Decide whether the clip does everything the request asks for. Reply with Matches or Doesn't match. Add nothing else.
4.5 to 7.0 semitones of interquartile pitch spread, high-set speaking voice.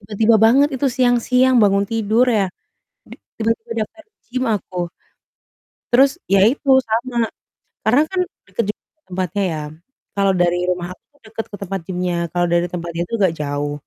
Matches